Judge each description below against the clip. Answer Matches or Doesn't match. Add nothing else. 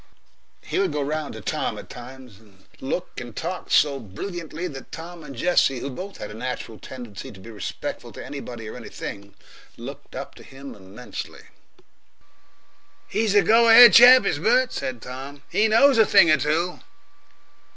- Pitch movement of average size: Doesn't match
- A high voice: Doesn't match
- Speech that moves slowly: Doesn't match